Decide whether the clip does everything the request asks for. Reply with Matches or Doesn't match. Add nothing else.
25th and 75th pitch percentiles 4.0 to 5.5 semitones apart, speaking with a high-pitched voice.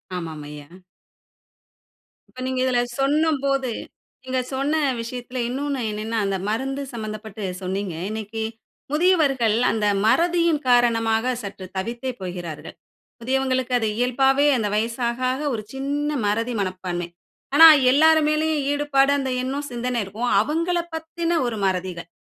Matches